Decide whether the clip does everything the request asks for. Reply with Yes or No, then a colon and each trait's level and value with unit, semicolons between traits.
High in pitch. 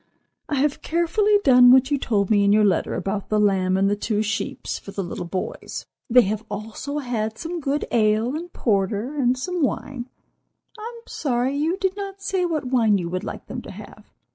Yes: high, 245 Hz